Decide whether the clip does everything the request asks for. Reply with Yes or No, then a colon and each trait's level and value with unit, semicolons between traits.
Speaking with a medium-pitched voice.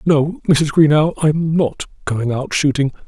Yes: medium, 145 Hz